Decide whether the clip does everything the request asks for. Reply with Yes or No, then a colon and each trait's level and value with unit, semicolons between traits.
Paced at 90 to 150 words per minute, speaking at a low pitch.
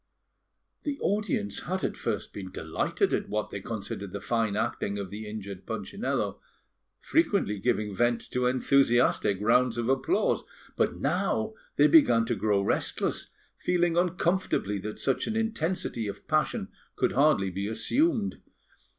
Yes: average, 140 wpm; low, 120 Hz